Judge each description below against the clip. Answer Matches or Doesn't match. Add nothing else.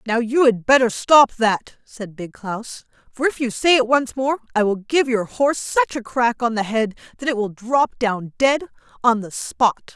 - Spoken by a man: Doesn't match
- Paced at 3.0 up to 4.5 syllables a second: Matches